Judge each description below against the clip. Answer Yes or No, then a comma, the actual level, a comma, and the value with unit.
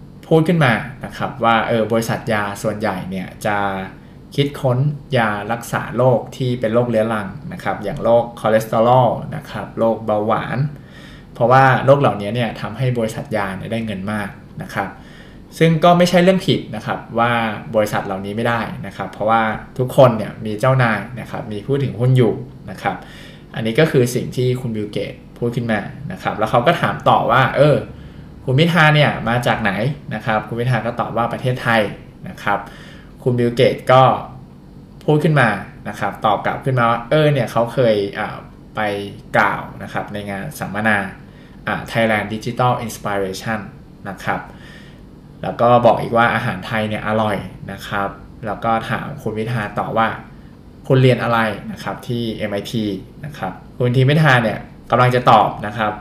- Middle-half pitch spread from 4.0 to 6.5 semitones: No, average, 3.4 semitones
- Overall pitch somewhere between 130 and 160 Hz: No, low, 115 Hz